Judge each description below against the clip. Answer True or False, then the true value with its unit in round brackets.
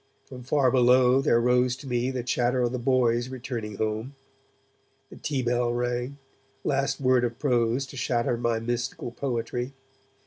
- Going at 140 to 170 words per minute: True (160 wpm)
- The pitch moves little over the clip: True (1.4 semitones)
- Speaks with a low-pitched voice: True (125 Hz)